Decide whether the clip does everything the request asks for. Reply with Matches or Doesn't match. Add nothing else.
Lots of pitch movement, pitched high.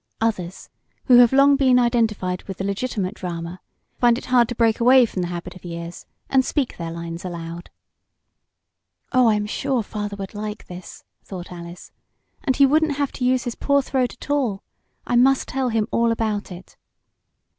Matches